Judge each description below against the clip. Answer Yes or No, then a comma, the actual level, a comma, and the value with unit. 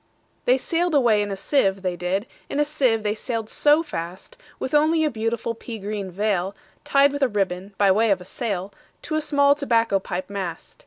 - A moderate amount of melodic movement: No, wide, 6.4 semitones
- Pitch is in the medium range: No, high, 220 Hz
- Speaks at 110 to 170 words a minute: No, average, 180 wpm